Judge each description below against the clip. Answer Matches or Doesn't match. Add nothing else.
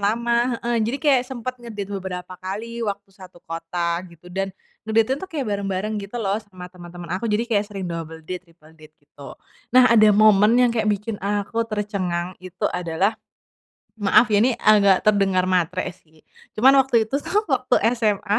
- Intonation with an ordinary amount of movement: Matches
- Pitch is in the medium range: Doesn't match